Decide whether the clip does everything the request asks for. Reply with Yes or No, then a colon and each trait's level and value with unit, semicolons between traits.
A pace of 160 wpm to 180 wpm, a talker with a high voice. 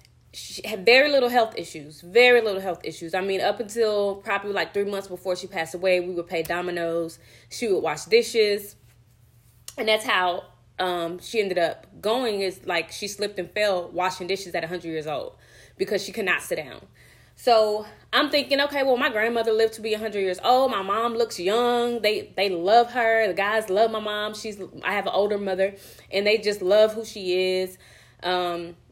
No: average, 200 wpm; high, 200 Hz